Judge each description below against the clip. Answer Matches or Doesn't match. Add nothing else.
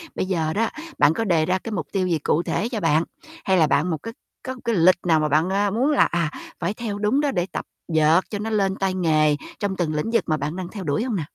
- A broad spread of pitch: Doesn't match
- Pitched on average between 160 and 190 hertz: Matches